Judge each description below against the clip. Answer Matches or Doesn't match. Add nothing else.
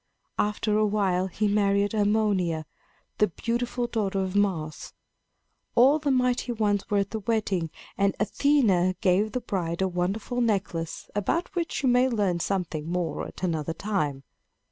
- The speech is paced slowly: Doesn't match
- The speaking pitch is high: Matches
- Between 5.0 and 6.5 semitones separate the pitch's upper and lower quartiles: Doesn't match